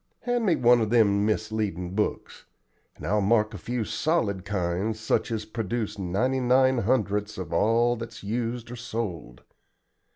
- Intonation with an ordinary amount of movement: Yes, average, 3.1 semitones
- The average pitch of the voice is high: No, low, 110 Hz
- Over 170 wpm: No, average, 155 wpm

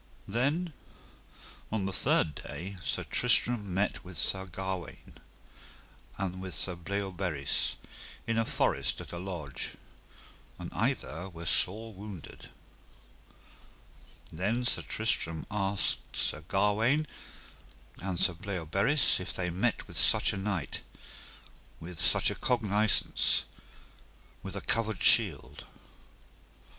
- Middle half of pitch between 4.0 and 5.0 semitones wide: No, average, 3.5 semitones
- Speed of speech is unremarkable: No, slow, 110 wpm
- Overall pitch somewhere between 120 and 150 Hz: No, very low, 95 Hz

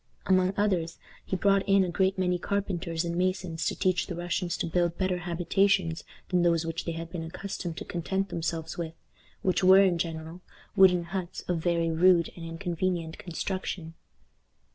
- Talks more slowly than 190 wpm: Yes, average, 170 wpm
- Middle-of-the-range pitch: Yes, medium, 175 Hz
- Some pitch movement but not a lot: No, narrow, 2.0 semitones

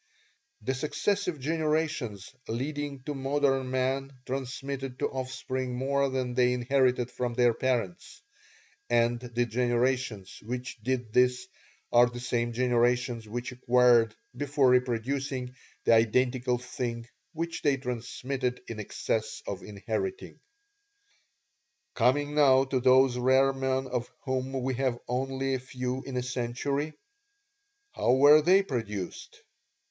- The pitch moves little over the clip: Yes, narrow, 1.7 semitones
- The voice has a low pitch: Yes, low, 130 Hz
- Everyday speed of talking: No, slow, 120 wpm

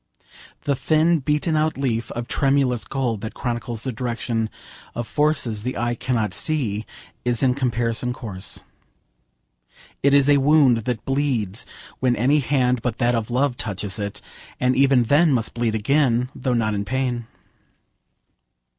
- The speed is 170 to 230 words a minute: No, average, 150 wpm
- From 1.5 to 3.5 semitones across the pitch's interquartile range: Yes, average, 3.2 semitones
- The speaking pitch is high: No, low, 125 Hz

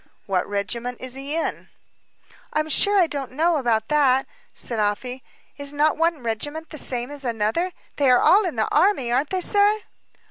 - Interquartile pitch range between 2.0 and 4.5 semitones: No, average, 5.0 semitones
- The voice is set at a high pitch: Yes, very high, 280 Hz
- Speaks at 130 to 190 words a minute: Yes, average, 180 wpm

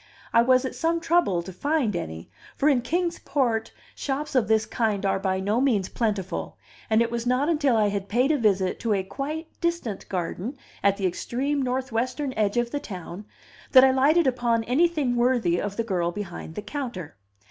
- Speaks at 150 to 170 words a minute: No, average, 190 wpm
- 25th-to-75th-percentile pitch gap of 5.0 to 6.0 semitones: Yes, average, 5.3 semitones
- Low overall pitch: No, high, 235 Hz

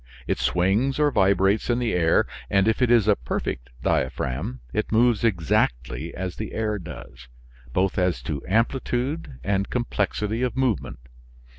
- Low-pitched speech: Yes, low, 100 Hz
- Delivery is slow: No, average, 150 wpm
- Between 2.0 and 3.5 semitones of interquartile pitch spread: No, average, 5.0 semitones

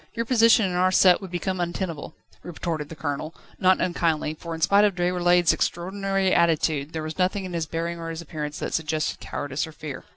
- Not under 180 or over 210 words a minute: Yes, average, 200 wpm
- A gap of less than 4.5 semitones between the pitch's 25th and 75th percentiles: Yes, average, 2.9 semitones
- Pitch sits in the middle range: Yes, medium, 170 Hz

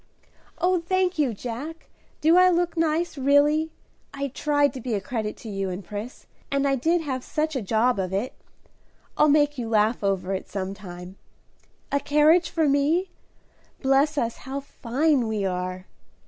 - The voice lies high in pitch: Yes, very high, 275 Hz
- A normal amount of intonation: No, wide, 6.4 semitones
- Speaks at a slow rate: No, average, 170 wpm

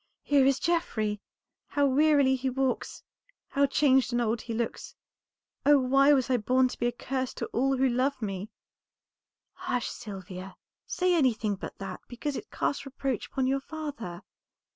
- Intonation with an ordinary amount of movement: Yes, average, 3.2 semitones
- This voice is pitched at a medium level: No, very high, 260 Hz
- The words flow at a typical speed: Yes, average, 165 wpm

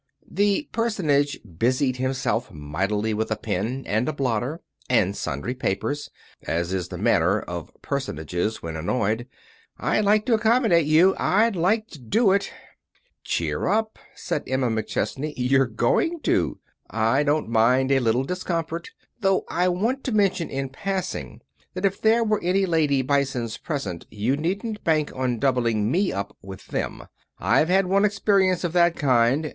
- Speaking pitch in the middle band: Yes, medium, 145 Hz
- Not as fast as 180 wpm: Yes, average, 155 wpm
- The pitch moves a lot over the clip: Yes, wide, 8.5 semitones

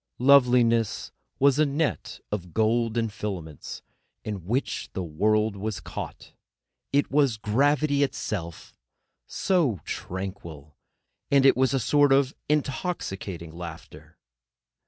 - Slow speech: Yes, slow, 110 wpm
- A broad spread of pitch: Yes, wide, 6.5 semitones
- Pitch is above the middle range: No, low, 115 Hz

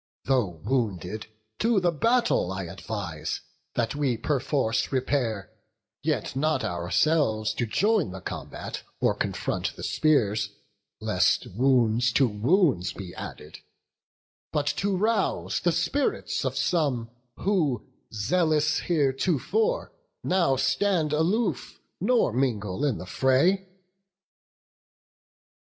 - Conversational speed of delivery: No, slow, 105 wpm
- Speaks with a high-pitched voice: No, low, 135 Hz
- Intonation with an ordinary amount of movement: No, wide, 7.7 semitones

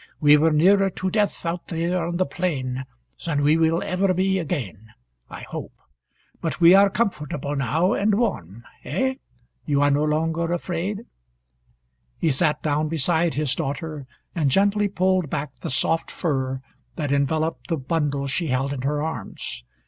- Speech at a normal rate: Yes, average, 160 wpm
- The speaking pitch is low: No, medium, 160 Hz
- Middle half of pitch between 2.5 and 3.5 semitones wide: No, average, 4.1 semitones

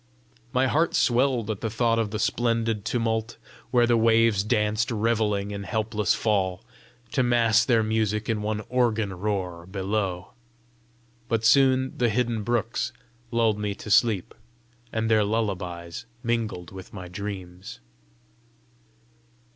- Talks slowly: Yes, slow, 130 wpm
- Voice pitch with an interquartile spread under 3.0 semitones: Yes, narrow, 2.5 semitones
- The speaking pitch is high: No, low, 110 Hz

